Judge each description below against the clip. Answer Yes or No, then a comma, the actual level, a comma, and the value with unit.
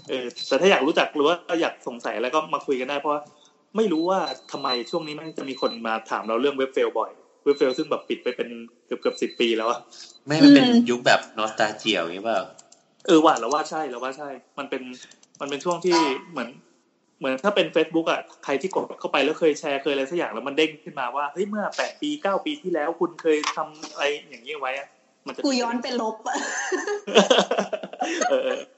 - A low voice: No, medium, 155 Hz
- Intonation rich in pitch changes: Yes, wide, 7.6 semitones